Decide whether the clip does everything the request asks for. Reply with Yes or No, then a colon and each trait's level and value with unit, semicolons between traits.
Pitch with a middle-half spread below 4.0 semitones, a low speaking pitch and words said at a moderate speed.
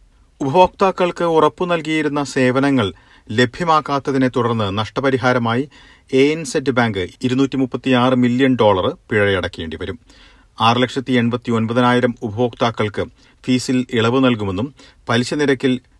Yes: narrow, 2.4 semitones; low, 130 Hz; average, 80 wpm